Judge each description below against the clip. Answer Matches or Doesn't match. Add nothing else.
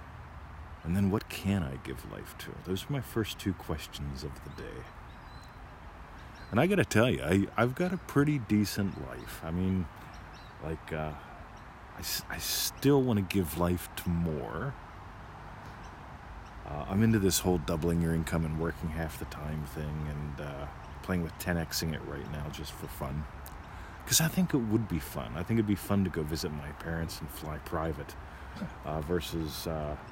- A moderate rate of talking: Matches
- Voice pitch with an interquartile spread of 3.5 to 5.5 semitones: Matches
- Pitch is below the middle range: Matches